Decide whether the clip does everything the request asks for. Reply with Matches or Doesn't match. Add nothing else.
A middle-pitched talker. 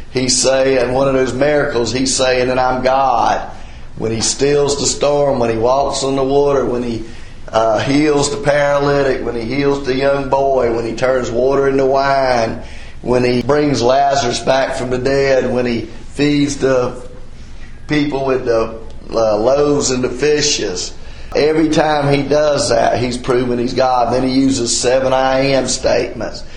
Doesn't match